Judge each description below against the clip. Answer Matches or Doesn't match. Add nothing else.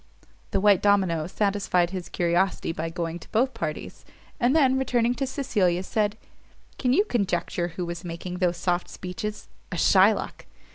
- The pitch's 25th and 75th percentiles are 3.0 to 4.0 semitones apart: Doesn't match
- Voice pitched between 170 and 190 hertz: Matches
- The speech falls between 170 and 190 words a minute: Doesn't match